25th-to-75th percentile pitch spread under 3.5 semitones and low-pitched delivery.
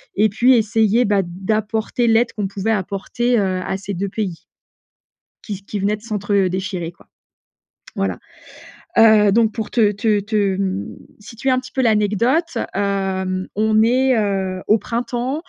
No: average, 2.8 semitones; high, 210 Hz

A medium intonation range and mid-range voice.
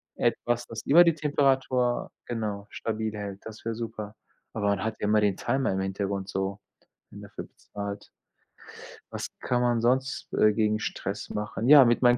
No: average, 3.2 semitones; low, 110 Hz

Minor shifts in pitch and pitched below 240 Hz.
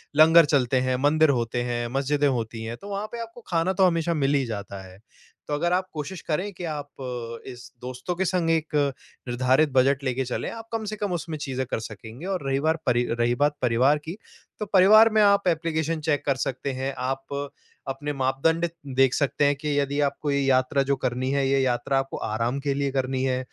No: average, 4.1 semitones; medium, 140 Hz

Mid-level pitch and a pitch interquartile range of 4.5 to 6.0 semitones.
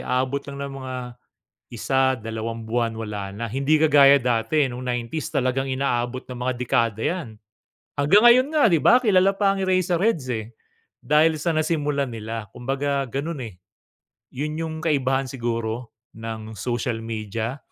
No: low, 130 Hz; average, 4.8 semitones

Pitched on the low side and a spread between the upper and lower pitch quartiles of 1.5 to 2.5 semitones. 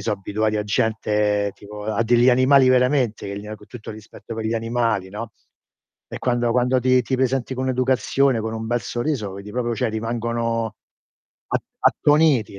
No: low, 115 Hz; average, 2.9 semitones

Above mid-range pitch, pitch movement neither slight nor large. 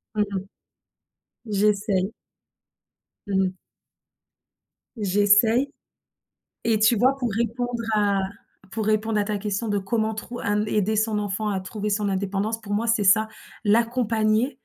No: high, 215 Hz; narrow, 1.8 semitones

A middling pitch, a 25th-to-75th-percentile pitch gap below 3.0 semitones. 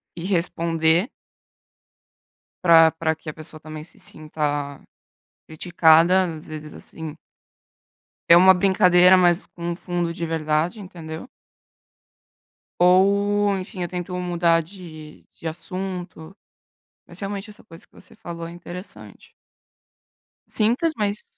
Yes: medium, 175 Hz; narrow, 2.6 semitones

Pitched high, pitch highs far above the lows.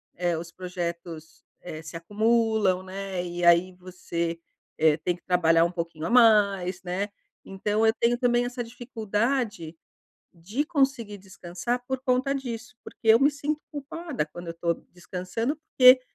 Yes: high, 195 Hz; wide, 5.8 semitones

